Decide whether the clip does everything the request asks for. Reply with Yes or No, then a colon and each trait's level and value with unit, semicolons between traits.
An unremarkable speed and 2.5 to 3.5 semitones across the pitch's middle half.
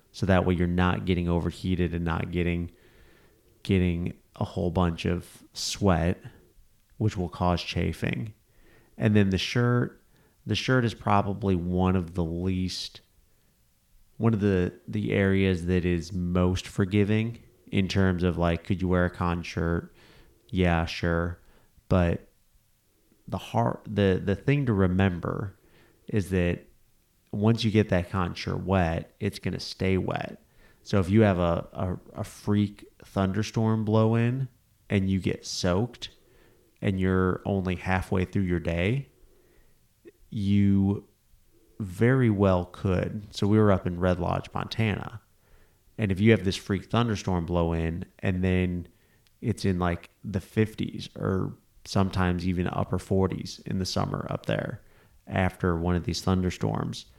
Yes: average, 145 wpm; average, 3.0 semitones